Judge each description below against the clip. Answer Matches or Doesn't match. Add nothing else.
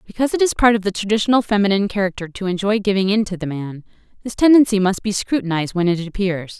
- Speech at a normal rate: Doesn't match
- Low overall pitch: Doesn't match